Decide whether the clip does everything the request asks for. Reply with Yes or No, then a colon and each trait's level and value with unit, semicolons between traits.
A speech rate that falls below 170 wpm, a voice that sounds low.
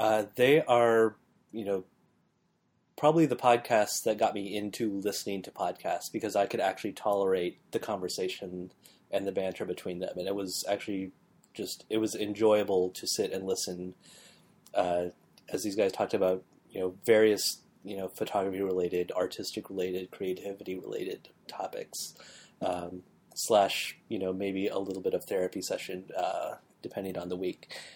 Yes: average, 155 wpm; low, 100 Hz